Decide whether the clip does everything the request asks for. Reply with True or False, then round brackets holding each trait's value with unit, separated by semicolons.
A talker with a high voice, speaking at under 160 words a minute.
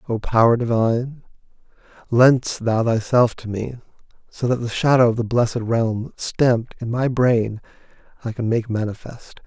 False (115 Hz; 150 wpm)